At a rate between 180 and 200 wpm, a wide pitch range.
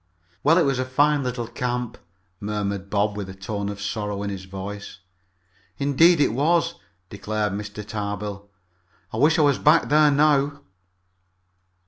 No: average, 150 wpm; wide, 5.9 semitones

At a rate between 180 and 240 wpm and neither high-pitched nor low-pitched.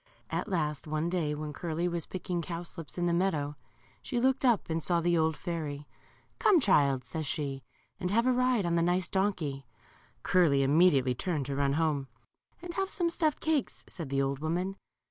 Yes: average, 190 wpm; medium, 170 Hz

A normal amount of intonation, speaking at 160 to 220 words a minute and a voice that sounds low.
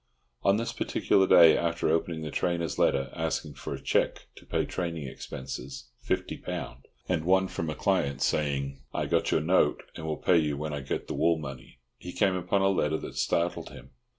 Yes: average, 3.6 semitones; average, 190 wpm; very low, 80 Hz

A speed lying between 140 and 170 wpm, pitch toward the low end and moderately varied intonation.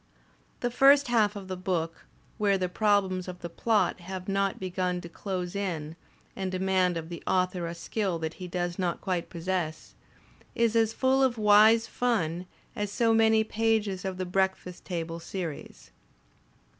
No: average, 165 wpm; high, 190 Hz; average, 3.3 semitones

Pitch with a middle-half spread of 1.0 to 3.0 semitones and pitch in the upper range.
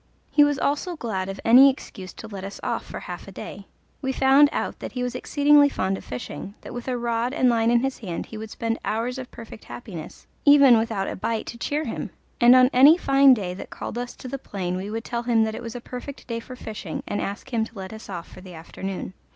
No: average, 4.4 semitones; high, 235 Hz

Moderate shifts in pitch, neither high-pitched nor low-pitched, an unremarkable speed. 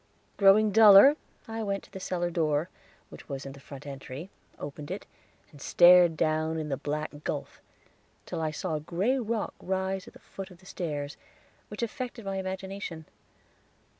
Yes: average, 4.4 semitones; medium, 180 Hz; average, 170 wpm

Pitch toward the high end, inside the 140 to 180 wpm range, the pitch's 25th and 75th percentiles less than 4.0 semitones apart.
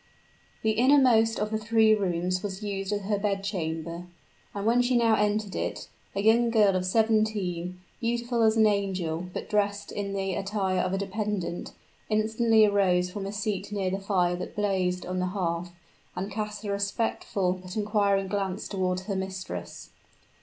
Yes: high, 200 Hz; average, 170 wpm; narrow, 2.6 semitones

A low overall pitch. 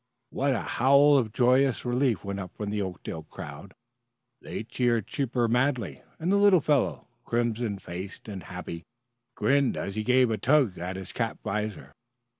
Yes: low, 115 Hz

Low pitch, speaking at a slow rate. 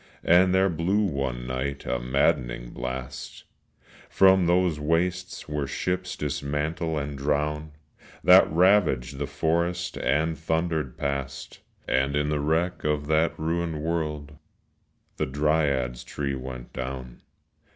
Yes: very low, 75 Hz; slow, 120 wpm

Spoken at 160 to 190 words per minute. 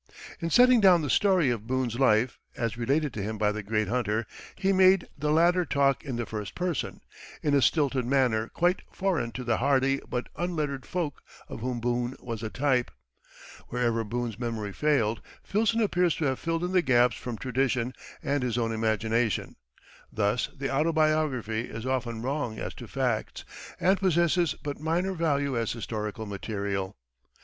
Yes: average, 170 wpm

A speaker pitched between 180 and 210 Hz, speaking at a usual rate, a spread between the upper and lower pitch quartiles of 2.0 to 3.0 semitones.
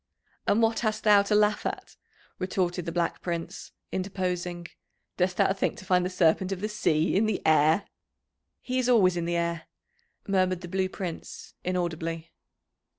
Yes: medium, 185 Hz; average, 165 wpm; average, 2.7 semitones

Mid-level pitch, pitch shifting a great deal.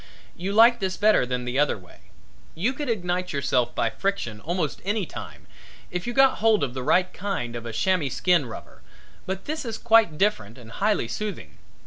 Yes: medium, 180 Hz; wide, 8.8 semitones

